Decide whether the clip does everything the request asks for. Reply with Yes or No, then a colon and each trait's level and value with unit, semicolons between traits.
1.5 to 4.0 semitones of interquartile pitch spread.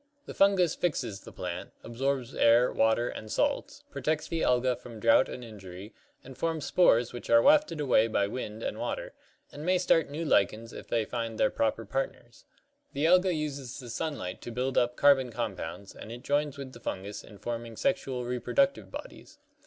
No: average, 5.0 semitones